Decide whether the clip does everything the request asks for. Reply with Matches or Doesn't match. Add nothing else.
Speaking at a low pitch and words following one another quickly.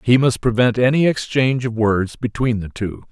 Doesn't match